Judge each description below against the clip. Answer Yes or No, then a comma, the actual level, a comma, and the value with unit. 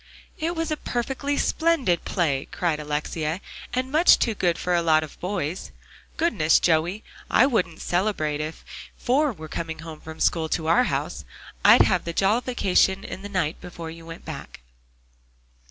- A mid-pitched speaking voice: Yes, medium, 175 Hz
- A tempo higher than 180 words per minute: No, average, 165 wpm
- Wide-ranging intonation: Yes, wide, 7.0 semitones